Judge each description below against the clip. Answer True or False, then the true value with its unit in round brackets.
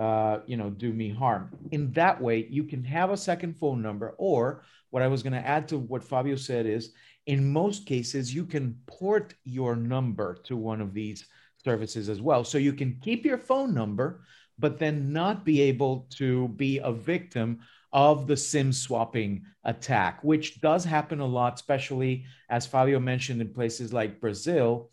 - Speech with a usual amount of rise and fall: True (4.3 semitones)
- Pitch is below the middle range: True (130 Hz)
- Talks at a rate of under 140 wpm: False (185 wpm)